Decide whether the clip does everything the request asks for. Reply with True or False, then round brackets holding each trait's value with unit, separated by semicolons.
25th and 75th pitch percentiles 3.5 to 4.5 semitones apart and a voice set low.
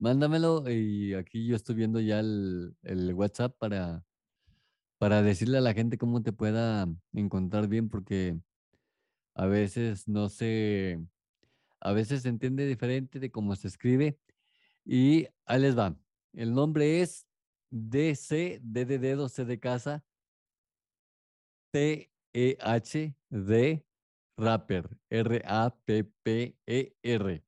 True (4.1 semitones; 115 Hz)